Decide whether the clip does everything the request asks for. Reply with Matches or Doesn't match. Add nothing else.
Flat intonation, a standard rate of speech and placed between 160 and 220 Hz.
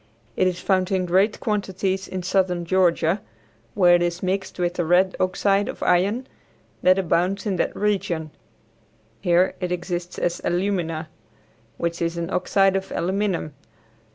Matches